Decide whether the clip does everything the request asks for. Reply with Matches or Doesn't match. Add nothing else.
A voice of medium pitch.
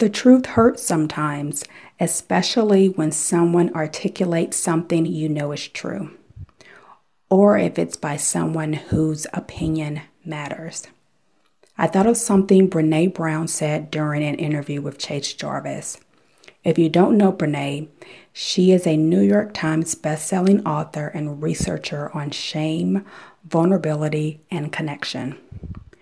Matches